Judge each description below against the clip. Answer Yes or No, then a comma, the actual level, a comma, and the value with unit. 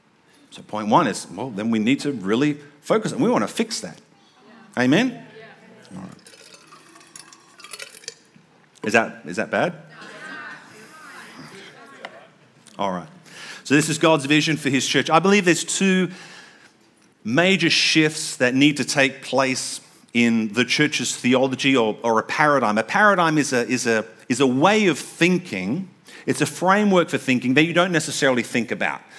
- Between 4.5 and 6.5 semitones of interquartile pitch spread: Yes, average, 5.0 semitones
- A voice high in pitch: No, medium, 150 Hz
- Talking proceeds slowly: No, average, 155 wpm